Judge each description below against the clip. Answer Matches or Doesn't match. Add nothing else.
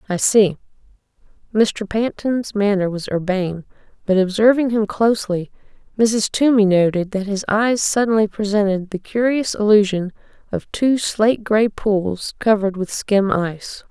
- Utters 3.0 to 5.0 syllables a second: Matches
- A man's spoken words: Doesn't match